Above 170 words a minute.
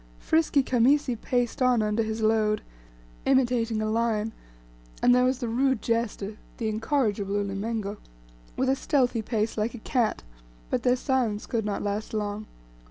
No: average, 155 wpm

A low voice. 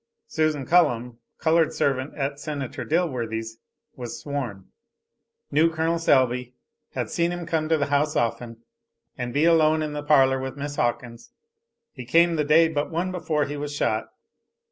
No: medium, 145 Hz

